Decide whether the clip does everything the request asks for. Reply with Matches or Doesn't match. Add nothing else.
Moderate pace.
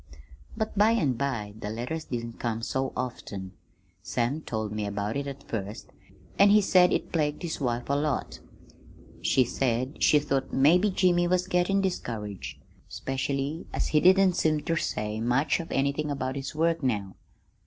Matches